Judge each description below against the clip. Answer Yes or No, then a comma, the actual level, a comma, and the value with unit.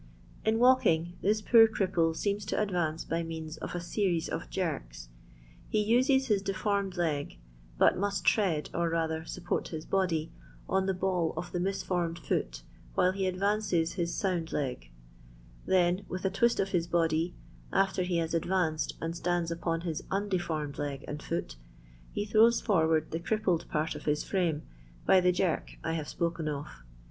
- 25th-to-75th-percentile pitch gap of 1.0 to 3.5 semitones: Yes, average, 3.2 semitones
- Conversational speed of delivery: Yes, average, 170 wpm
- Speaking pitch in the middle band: Yes, medium, 175 Hz